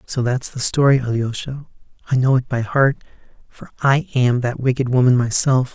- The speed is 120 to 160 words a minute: No, average, 180 wpm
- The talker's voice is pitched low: Yes, low, 125 Hz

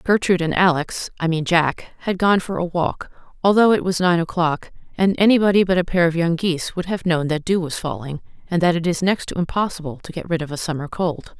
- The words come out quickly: Yes, fast, 225 wpm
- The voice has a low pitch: No, medium, 175 Hz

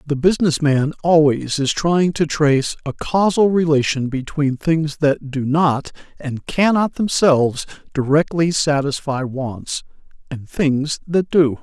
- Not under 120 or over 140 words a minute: Yes, slow, 135 wpm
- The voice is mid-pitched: Yes, medium, 150 Hz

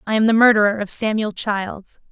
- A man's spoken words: No, female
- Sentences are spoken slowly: No, average, 200 wpm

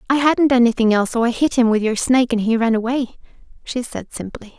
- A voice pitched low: No, high, 240 Hz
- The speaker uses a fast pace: Yes, fast, 235 wpm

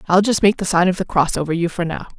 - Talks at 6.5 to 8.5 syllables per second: Yes, 6.7 syllables/s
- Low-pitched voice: No, medium, 180 Hz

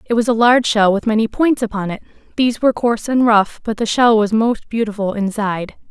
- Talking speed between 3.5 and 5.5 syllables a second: No, 6.0 syllables/s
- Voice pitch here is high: Yes, high, 220 Hz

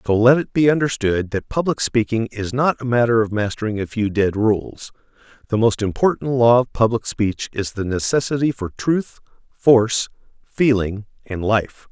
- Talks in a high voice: No, low, 115 Hz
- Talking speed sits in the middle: Yes, average, 170 wpm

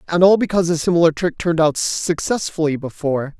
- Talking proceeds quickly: No, average, 175 wpm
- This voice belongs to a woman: No, male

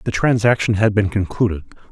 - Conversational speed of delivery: Yes, average, 155 wpm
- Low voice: Yes, low, 105 Hz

